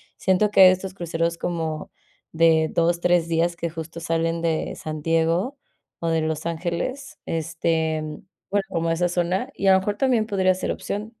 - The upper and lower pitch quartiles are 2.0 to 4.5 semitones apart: Yes, narrow, 2.4 semitones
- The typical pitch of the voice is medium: Yes, medium, 170 Hz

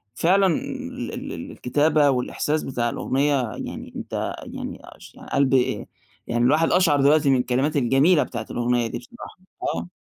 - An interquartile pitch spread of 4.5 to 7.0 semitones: No, average, 3.6 semitones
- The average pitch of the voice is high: No, low, 135 Hz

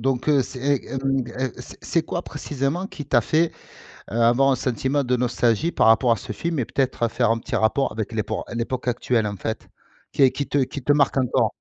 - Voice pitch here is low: Yes, low, 130 Hz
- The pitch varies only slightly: No, average, 3.2 semitones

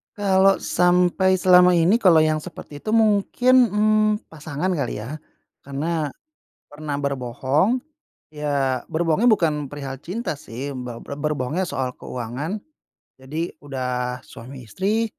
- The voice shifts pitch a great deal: Yes, wide, 5.8 semitones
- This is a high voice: No, medium, 155 Hz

